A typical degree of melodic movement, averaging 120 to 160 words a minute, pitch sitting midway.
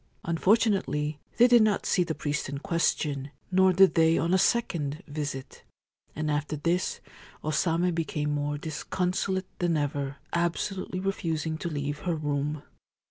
Yes: average, 3.7 semitones; average, 145 wpm; medium, 160 Hz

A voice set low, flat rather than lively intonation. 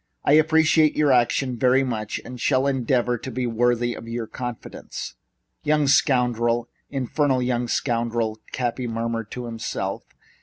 Yes: low, 125 Hz; narrow, 2.3 semitones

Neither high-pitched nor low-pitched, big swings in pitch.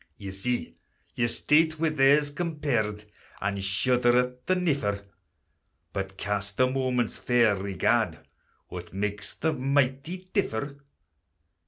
No: low, 125 Hz; wide, 6.0 semitones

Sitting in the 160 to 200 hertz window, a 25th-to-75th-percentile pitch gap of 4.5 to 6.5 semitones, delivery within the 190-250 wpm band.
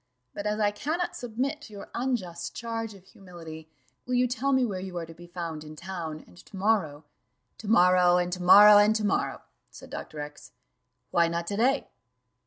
Yes: high, 190 Hz; average, 4.8 semitones; average, 200 wpm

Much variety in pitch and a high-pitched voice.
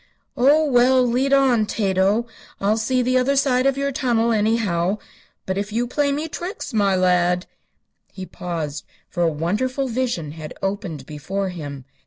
Yes: wide, 6.2 semitones; high, 220 Hz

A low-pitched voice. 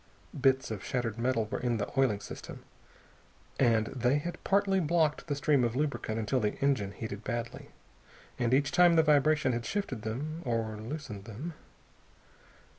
Yes: low, 130 Hz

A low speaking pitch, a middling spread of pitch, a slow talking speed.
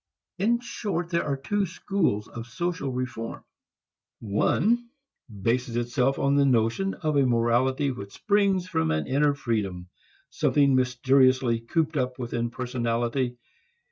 Yes: low, 130 Hz; average, 4.6 semitones; slow, 130 wpm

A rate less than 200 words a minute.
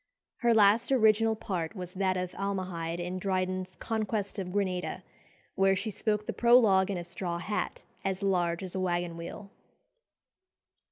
Yes: average, 155 wpm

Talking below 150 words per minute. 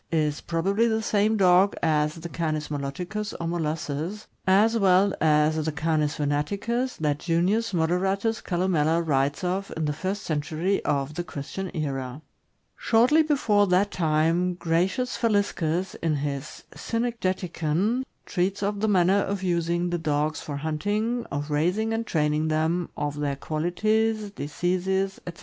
Yes: average, 140 wpm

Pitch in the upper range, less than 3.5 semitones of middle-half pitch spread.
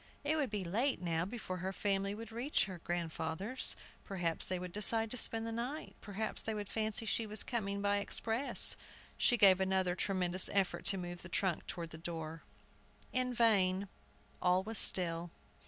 No: high, 195 Hz; average, 3.9 semitones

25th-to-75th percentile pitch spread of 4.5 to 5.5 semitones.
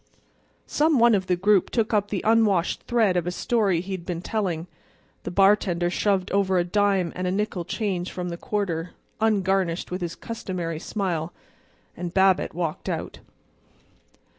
No: average, 2.9 semitones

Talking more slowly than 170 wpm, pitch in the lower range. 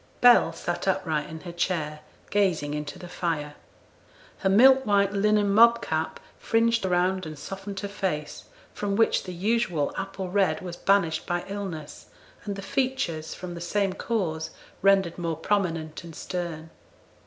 No: average, 155 wpm; medium, 185 Hz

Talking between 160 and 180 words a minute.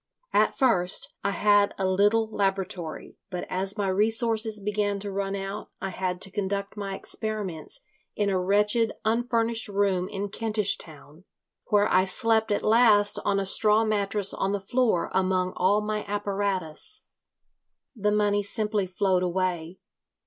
No: average, 150 wpm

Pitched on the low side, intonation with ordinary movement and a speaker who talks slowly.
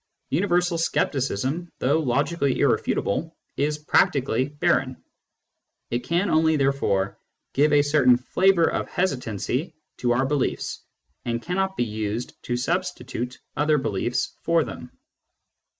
No: medium, 145 Hz; average, 5.0 semitones; slow, 120 wpm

